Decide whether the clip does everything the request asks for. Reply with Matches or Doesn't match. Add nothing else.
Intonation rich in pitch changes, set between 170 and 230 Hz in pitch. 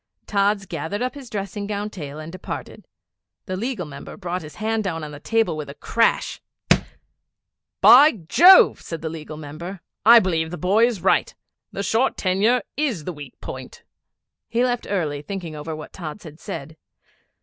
Matches